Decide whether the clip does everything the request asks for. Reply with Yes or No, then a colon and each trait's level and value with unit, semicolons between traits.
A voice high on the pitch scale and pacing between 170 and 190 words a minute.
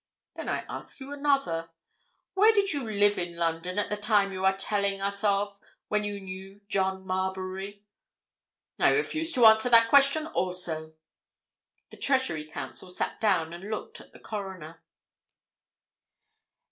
No: high, 200 Hz; average, 145 wpm